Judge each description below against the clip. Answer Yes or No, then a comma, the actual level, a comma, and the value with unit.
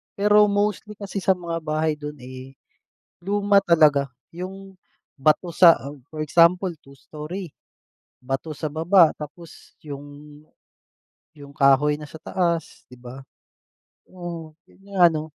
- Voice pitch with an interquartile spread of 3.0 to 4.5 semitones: Yes, average, 3.8 semitones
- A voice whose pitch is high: No, medium, 160 Hz